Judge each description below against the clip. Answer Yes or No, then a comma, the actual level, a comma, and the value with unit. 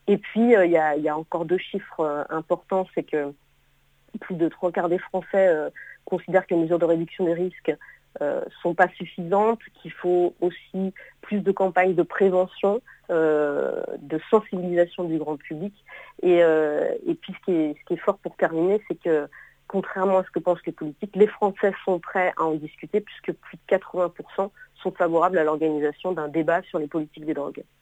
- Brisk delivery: No, average, 200 wpm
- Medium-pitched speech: Yes, medium, 180 Hz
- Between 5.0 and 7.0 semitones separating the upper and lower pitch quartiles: No, average, 3.0 semitones